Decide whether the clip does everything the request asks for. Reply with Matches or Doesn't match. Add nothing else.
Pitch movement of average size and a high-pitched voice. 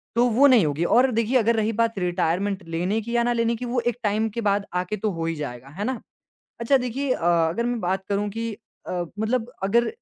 Matches